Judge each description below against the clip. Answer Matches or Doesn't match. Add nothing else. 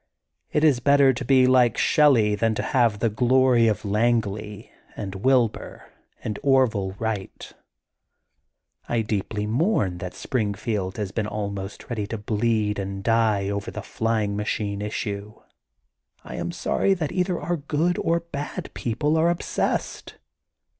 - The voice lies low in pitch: Matches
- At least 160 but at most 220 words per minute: Doesn't match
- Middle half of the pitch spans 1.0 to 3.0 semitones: Doesn't match